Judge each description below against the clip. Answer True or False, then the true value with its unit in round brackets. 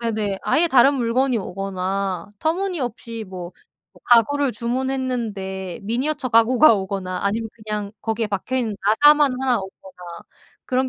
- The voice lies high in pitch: True (230 Hz)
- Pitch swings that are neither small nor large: True (4.7 semitones)